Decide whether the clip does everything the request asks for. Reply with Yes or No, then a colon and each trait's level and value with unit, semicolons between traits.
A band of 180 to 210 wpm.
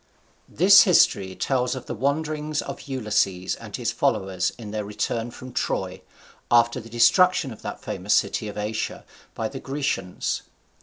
No: average, 155 wpm